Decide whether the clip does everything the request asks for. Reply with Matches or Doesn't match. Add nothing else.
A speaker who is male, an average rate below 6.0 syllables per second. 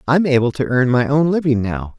Matches